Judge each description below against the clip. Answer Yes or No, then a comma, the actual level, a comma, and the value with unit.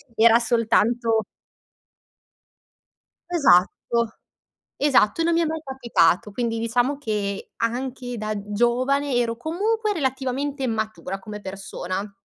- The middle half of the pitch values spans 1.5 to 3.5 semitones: No, average, 4.2 semitones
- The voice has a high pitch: Yes, high, 235 Hz